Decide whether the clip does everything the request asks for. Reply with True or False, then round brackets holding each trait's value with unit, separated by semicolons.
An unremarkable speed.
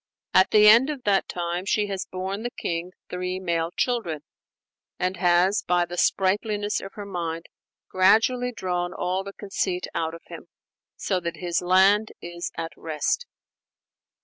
True (155 wpm)